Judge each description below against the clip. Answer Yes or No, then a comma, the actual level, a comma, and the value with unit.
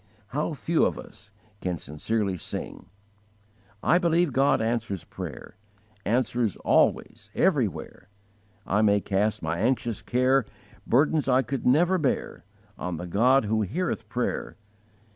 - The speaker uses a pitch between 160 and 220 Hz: No, low, 120 Hz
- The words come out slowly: Yes, slow, 125 wpm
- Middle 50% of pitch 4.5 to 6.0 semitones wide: Yes, average, 4.9 semitones